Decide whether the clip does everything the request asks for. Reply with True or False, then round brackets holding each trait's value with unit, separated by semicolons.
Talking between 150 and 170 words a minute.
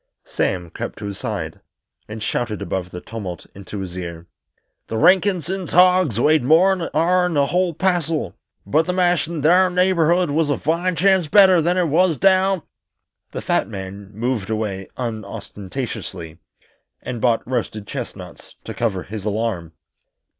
True (155 wpm)